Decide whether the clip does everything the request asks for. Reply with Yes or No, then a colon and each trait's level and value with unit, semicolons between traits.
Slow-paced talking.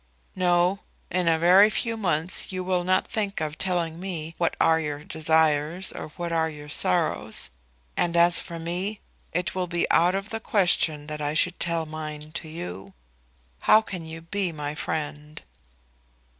No: average, 165 wpm